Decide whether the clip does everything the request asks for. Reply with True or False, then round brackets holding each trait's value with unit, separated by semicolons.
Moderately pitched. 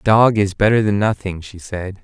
False (100 Hz)